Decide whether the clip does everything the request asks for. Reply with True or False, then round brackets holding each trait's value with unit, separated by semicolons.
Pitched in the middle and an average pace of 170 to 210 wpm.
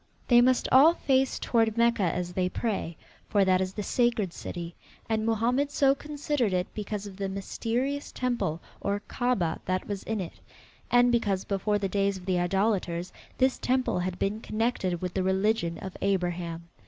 False (205 Hz; 175 wpm)